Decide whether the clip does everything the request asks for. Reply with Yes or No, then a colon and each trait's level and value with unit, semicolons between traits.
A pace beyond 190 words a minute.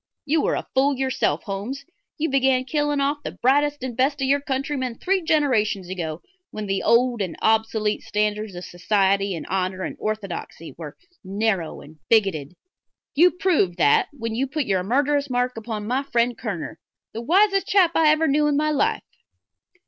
No: average, 175 wpm